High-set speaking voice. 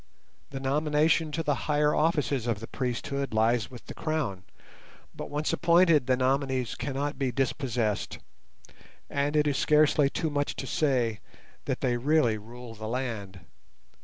No: low, 135 Hz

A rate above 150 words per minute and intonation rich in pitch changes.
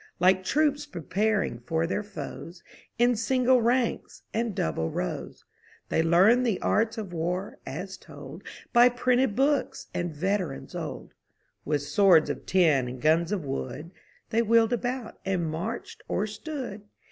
No: average, 145 wpm; wide, 6.4 semitones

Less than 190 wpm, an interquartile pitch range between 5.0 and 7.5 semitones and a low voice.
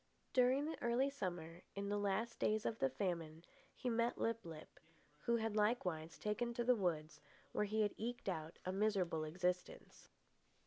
No: average, 170 wpm; average, 5.3 semitones; high, 205 Hz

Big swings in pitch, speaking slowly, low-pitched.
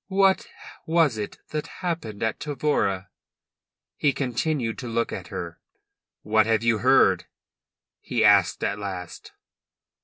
Yes: wide, 6.1 semitones; slow, 125 wpm; low, 115 Hz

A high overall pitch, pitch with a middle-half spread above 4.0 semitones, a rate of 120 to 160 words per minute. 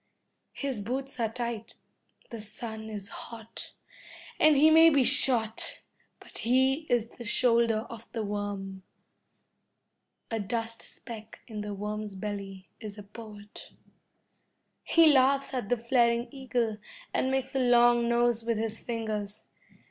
No: high, 230 Hz; average, 2.8 semitones; average, 140 wpm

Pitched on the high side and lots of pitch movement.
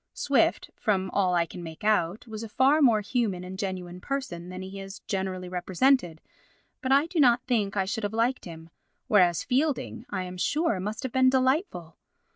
Yes: high, 200 Hz; wide, 5.9 semitones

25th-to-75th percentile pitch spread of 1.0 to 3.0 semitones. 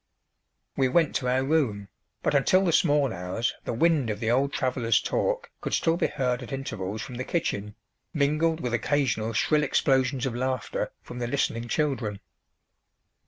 No: average, 4.1 semitones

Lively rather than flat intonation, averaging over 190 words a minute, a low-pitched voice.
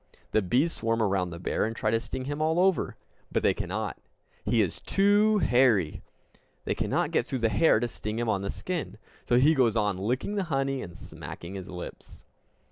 Yes: wide, 6.1 semitones; fast, 205 wpm; low, 115 Hz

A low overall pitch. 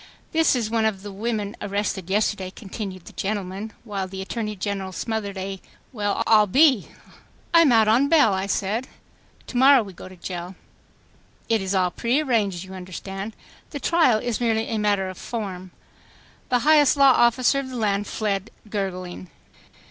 No: high, 210 Hz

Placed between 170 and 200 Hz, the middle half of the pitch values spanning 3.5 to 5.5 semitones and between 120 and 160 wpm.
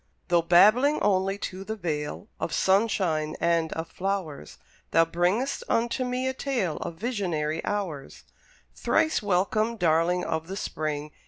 Yes: medium, 185 Hz; average, 4.8 semitones; average, 140 wpm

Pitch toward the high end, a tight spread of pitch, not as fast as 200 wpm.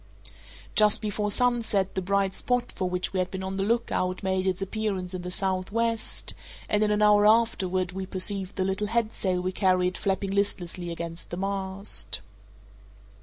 Yes: high, 195 Hz; narrow, 2.2 semitones; average, 170 wpm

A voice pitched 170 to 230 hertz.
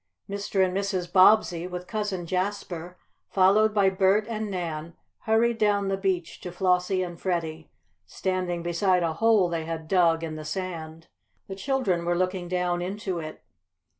Yes: medium, 185 Hz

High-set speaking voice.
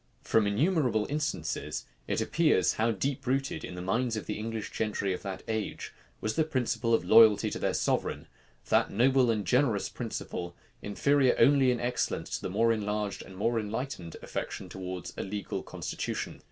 No: low, 115 Hz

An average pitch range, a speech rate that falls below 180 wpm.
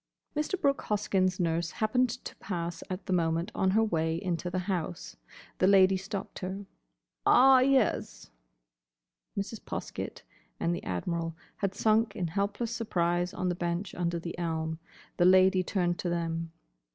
Yes: average, 3.2 semitones; average, 150 wpm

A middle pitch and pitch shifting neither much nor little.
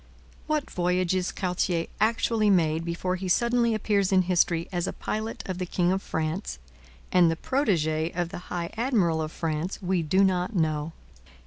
Yes: medium, 180 Hz; average, 3.0 semitones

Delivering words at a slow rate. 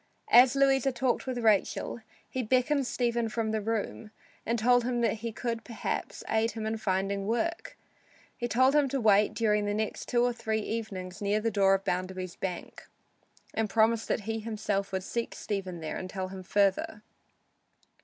No: average, 180 wpm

